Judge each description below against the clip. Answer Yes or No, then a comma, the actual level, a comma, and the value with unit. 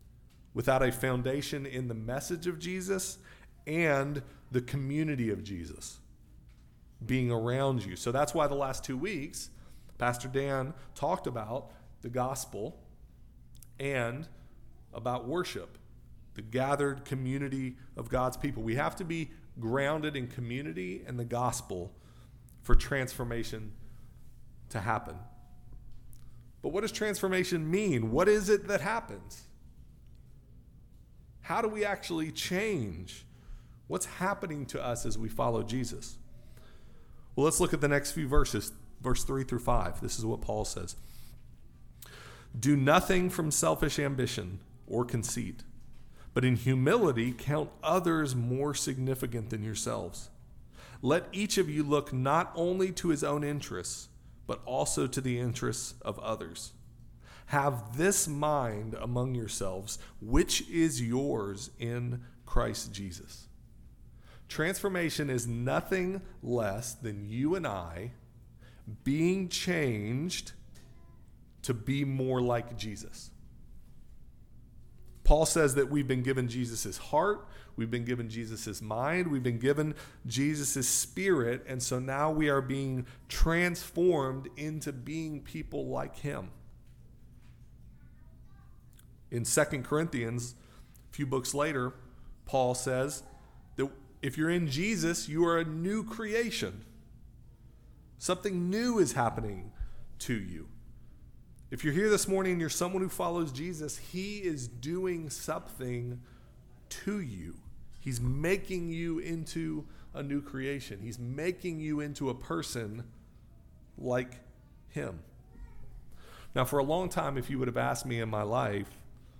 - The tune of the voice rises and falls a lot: No, average, 4.6 semitones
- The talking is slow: Yes, slow, 125 wpm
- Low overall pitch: Yes, low, 130 Hz